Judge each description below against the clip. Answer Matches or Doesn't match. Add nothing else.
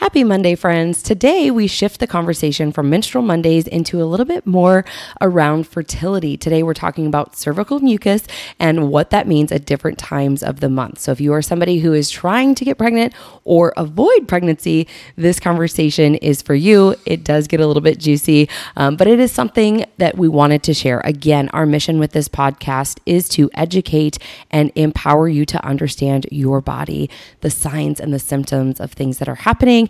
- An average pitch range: Matches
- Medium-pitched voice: Matches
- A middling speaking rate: Matches